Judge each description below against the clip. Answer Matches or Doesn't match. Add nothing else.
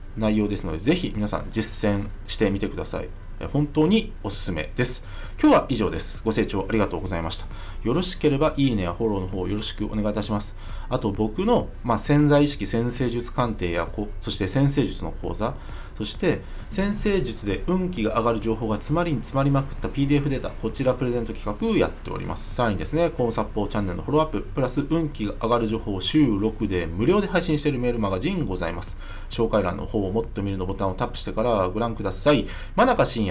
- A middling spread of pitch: Matches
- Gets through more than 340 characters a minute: Matches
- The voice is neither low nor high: Doesn't match